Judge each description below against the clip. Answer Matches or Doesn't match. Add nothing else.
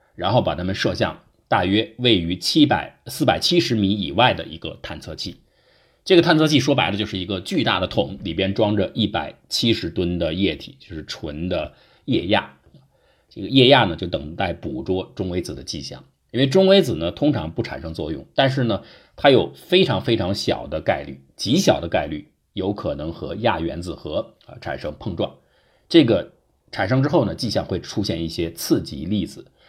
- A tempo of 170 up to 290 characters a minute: Matches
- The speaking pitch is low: Matches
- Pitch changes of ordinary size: Doesn't match